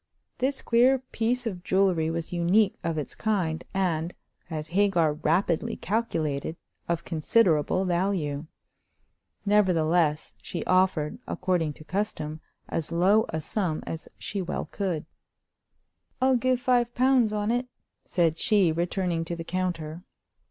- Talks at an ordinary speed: No, slow, 130 wpm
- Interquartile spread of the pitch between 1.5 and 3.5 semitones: No, average, 4.5 semitones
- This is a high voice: No, medium, 180 Hz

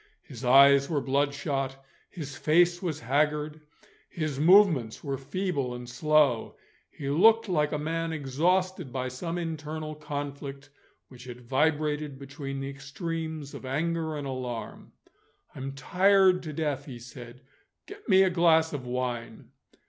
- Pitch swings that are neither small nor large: Yes, average, 3.3 semitones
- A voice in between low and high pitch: Yes, medium, 145 Hz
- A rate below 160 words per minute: Yes, average, 140 wpm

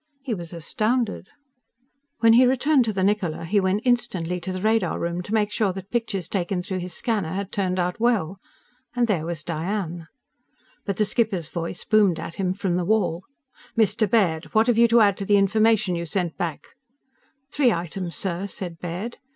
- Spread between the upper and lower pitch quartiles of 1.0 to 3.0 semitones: No, average, 3.9 semitones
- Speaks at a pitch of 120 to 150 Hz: No, high, 195 Hz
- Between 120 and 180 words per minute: No, average, 190 wpm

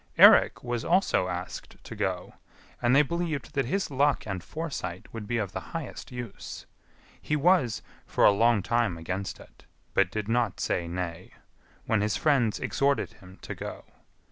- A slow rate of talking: No, average, 170 wpm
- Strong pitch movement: Yes, wide, 6.3 semitones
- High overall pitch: No, low, 115 Hz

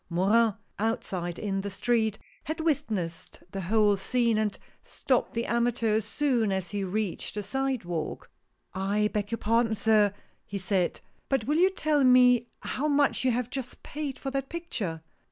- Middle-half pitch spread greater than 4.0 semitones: Yes, average, 4.5 semitones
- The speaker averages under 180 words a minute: Yes, average, 170 wpm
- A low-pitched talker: No, high, 225 Hz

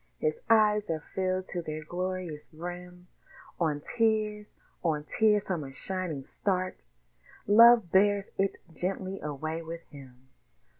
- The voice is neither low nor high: Yes, medium, 180 Hz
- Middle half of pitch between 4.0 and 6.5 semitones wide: Yes, average, 4.4 semitones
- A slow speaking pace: Yes, slow, 130 wpm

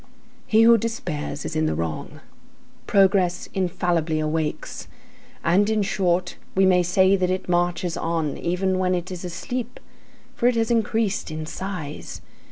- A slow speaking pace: No, average, 150 wpm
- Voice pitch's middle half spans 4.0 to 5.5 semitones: No, average, 2.8 semitones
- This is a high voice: No, medium, 180 Hz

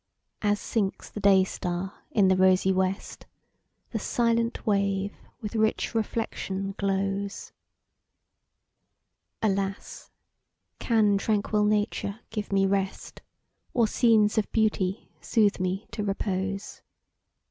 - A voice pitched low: No, high, 200 Hz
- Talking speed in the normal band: No, slow, 105 wpm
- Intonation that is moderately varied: No, narrow, 2.0 semitones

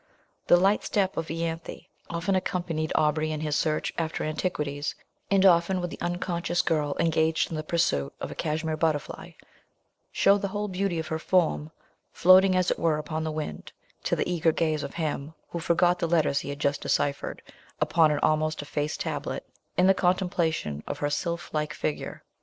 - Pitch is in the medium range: Yes, medium, 160 Hz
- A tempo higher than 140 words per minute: Yes, average, 180 wpm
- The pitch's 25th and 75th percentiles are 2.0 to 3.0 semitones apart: Yes, narrow, 2.4 semitones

